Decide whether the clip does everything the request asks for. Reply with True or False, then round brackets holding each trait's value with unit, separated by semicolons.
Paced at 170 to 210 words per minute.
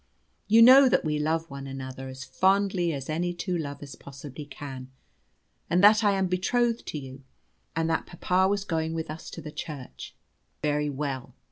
True (175 wpm)